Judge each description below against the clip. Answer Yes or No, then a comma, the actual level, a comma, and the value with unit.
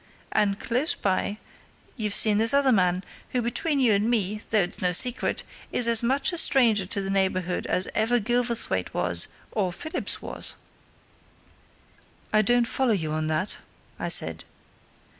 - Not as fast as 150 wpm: No, average, 160 wpm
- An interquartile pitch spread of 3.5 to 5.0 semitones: Yes, average, 4.5 semitones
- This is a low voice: No, high, 215 Hz